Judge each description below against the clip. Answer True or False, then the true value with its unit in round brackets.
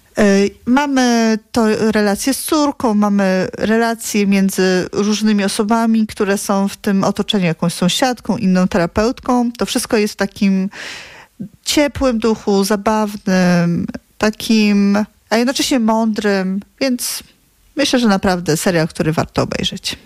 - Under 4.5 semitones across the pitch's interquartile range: True (2.8 semitones)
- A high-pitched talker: True (215 Hz)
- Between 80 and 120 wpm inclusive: True (115 wpm)